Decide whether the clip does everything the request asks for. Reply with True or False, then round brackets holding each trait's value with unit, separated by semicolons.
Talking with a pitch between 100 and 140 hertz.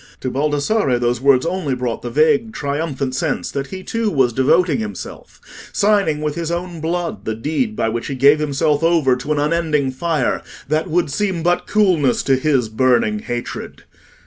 False (150 Hz)